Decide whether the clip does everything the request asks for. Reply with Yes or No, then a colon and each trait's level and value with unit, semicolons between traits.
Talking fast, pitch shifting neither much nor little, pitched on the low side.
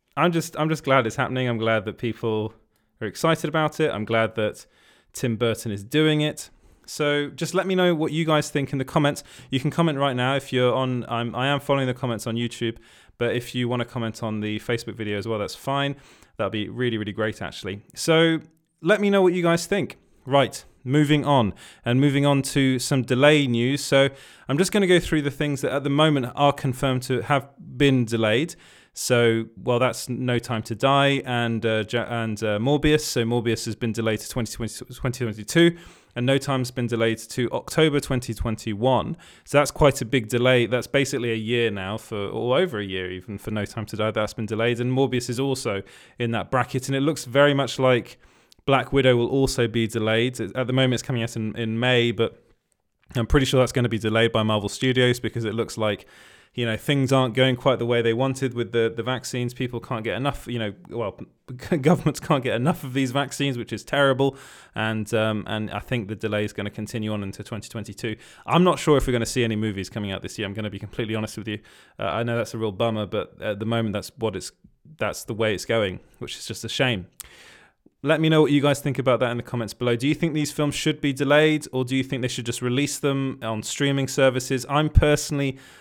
Yes: fast, 230 wpm; average, 3.8 semitones; low, 125 Hz